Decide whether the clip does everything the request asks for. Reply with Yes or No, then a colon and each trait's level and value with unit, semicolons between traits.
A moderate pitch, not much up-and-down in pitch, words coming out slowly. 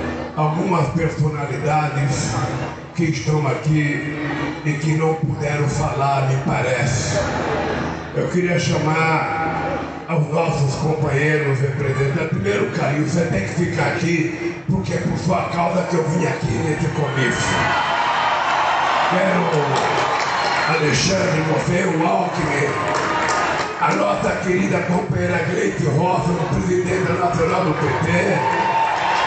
Yes: medium, 155 Hz; narrow, 2.2 semitones; slow, 110 wpm